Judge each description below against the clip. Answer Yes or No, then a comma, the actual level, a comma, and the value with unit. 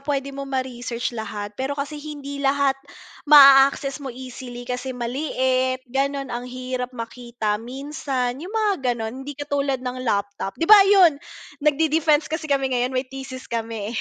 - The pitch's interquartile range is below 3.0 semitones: Yes, narrow, 2.5 semitones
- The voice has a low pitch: No, very high, 265 Hz